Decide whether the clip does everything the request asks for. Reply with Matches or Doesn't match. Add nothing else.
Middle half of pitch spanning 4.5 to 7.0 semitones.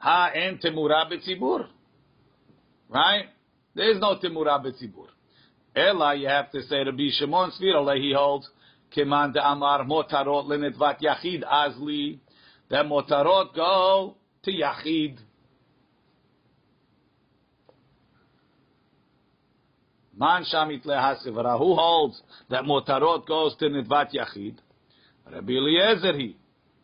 Doesn't match